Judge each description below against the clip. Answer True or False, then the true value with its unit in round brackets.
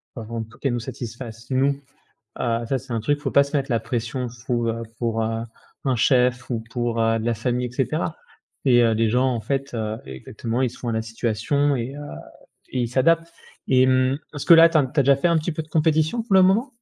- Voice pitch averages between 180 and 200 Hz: False (125 Hz)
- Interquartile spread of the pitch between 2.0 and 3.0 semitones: False (3.5 semitones)